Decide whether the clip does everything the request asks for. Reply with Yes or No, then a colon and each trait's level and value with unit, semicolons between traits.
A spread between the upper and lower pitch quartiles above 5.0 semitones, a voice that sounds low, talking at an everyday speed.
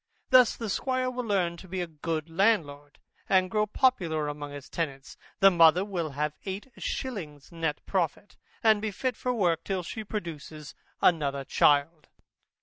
No: wide, 5.5 semitones; medium, 170 Hz; average, 160 wpm